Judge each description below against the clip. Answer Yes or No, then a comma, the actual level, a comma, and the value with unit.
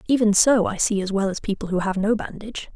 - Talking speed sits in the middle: No, fast, 260 wpm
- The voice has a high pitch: Yes, high, 205 Hz